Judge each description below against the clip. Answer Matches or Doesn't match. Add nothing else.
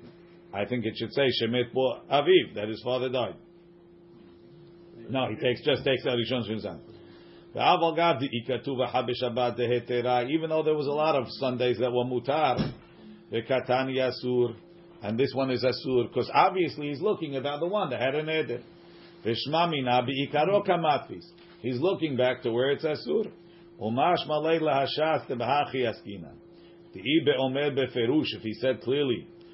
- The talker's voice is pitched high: Doesn't match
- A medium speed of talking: Matches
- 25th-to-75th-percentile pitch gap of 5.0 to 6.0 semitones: Matches